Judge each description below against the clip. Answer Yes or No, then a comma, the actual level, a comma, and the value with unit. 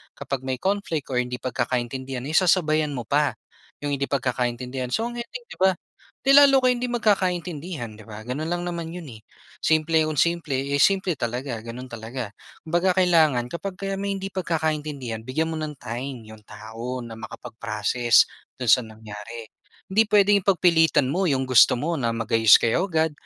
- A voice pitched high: No, medium, 145 Hz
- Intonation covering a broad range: Yes, wide, 6.4 semitones